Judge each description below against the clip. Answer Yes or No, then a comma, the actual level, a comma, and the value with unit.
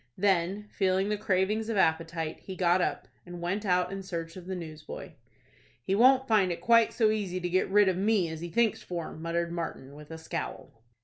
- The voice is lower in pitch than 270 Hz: Yes, medium, 185 Hz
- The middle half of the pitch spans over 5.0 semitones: No, average, 3.3 semitones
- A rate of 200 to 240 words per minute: Yes, fast, 205 wpm